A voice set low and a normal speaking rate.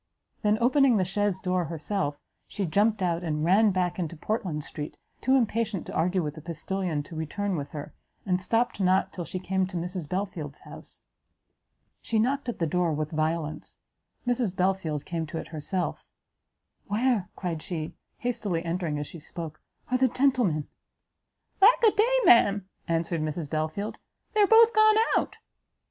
No: medium, 180 Hz; average, 165 wpm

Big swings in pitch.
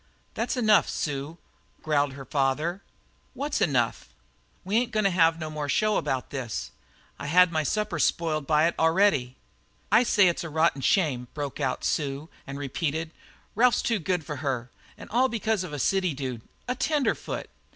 Yes: wide, 5.9 semitones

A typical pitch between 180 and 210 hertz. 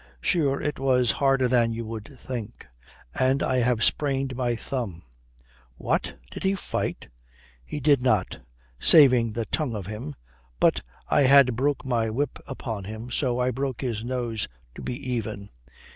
No: low, 125 Hz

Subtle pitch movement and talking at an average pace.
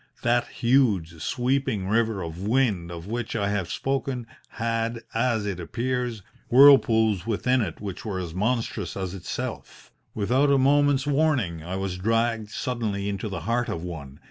No: average, 4.7 semitones; average, 155 wpm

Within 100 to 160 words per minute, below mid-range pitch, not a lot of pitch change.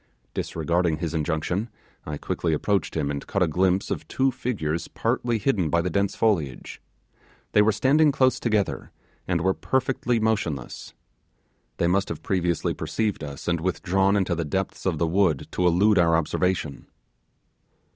No: average, 155 wpm; very low, 90 Hz; average, 4.2 semitones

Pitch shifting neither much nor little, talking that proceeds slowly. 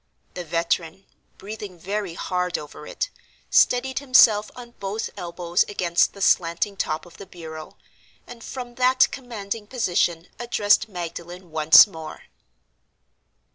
Yes: average, 4.7 semitones; slow, 125 wpm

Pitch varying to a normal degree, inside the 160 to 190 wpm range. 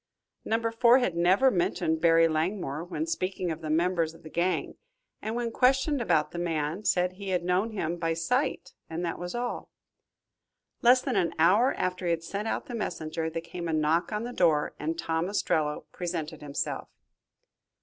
Yes: average, 4.6 semitones; average, 185 wpm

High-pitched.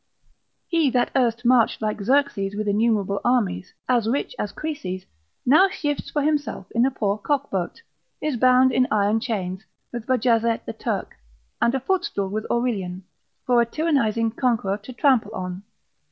Yes: high, 235 Hz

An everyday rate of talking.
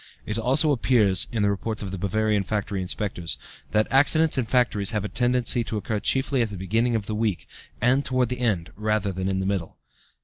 No: fast, 210 wpm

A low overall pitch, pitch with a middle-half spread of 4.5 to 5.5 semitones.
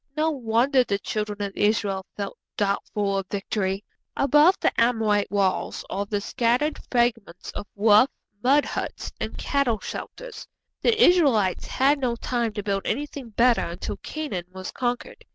No: high, 225 Hz; average, 5.2 semitones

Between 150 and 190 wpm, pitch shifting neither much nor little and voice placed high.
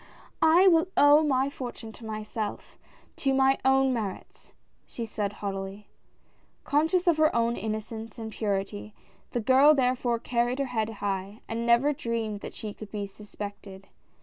Yes: average, 155 wpm; average, 4.2 semitones; high, 230 Hz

